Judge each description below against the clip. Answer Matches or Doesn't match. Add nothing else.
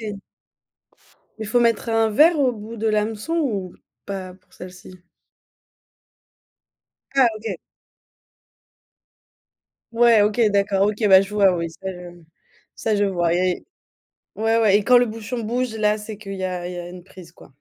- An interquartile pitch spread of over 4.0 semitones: Doesn't match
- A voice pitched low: Doesn't match